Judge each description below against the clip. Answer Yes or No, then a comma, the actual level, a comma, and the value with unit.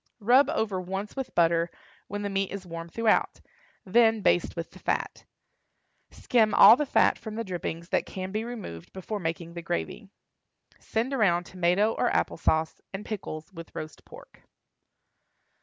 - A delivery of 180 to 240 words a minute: No, average, 160 wpm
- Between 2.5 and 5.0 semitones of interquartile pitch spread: Yes, average, 4.5 semitones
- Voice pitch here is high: Yes, high, 195 Hz